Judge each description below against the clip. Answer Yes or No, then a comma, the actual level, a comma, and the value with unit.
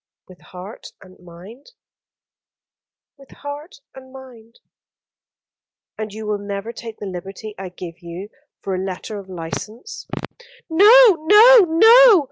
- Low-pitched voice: No, high, 220 Hz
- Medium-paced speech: No, slow, 125 wpm